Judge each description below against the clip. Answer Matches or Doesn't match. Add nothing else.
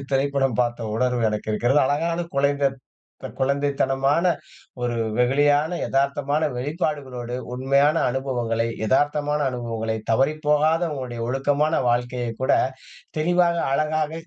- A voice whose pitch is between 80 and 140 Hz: Matches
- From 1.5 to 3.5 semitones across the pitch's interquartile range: Matches